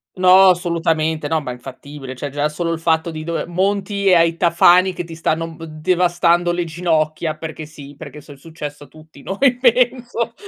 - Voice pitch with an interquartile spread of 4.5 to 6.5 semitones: No, average, 2.7 semitones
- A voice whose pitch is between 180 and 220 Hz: No, medium, 165 Hz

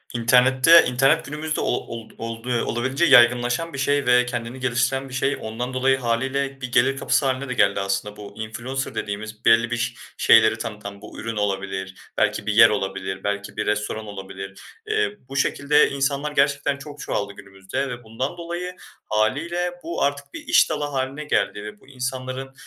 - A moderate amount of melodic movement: Yes, average, 4.1 semitones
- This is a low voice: Yes, low, 125 Hz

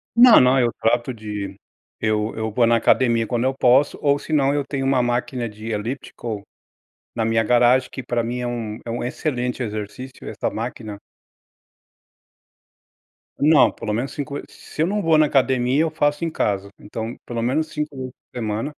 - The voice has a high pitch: No, low, 125 Hz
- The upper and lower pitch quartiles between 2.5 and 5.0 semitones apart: Yes, average, 3.6 semitones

